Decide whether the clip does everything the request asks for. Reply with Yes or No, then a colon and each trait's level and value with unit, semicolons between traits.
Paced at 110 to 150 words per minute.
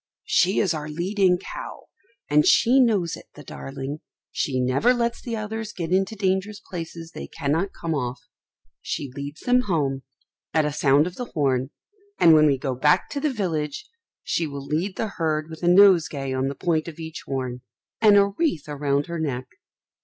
No: average, 185 wpm